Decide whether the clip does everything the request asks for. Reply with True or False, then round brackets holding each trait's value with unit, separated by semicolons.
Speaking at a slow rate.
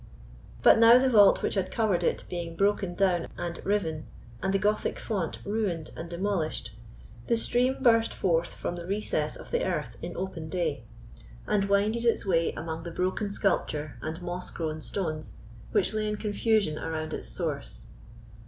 False (170 wpm)